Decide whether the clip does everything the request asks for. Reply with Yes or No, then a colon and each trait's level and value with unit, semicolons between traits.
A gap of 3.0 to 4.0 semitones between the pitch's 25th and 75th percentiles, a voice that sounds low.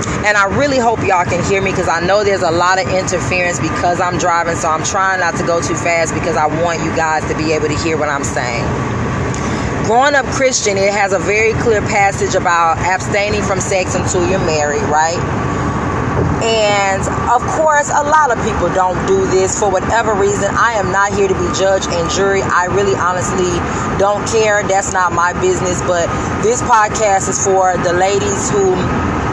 No: average, 3.3 semitones; medium, 185 Hz